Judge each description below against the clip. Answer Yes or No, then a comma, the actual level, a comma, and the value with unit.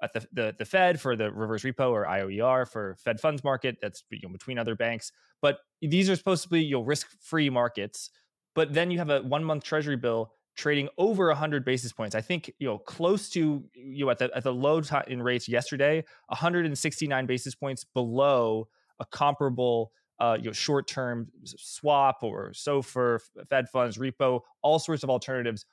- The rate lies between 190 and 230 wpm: Yes, average, 195 wpm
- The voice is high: No, low, 135 Hz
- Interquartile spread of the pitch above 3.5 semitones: Yes, average, 3.9 semitones